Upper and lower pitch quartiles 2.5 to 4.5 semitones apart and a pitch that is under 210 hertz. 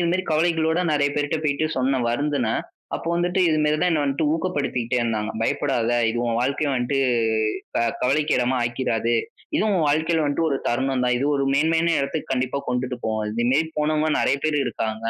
Yes: average, 4.1 semitones; medium, 140 Hz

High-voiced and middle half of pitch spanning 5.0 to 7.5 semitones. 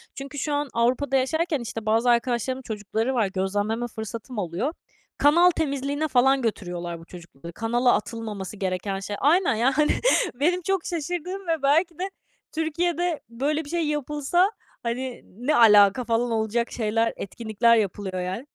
Yes: high, 245 Hz; wide, 5.6 semitones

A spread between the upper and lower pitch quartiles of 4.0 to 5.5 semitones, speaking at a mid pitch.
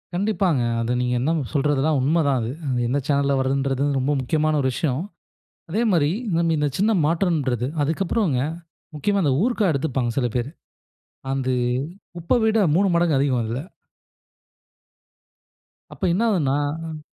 Yes: average, 4.4 semitones; medium, 145 Hz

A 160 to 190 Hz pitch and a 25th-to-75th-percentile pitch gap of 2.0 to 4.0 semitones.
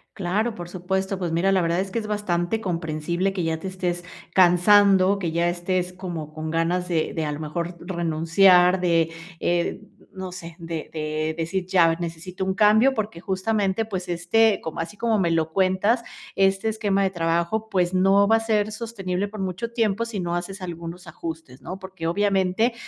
Yes: medium, 185 Hz; average, 2.7 semitones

